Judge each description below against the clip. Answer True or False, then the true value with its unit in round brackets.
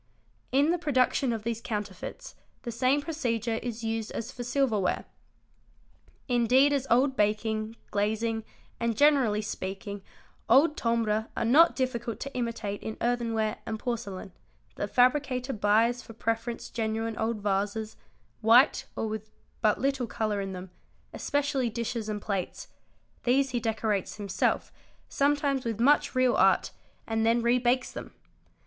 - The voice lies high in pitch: True (230 Hz)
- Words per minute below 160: True (140 wpm)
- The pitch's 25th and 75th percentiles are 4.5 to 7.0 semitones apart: False (2.9 semitones)